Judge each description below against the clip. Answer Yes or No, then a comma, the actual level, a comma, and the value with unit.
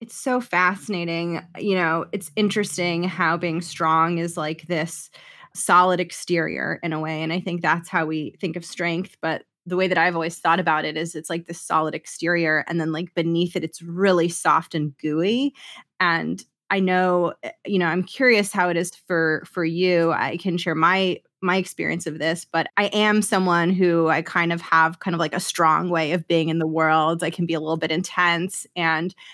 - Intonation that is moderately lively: No, narrow, 2.0 semitones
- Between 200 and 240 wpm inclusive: Yes, fast, 205 wpm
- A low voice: No, medium, 170 Hz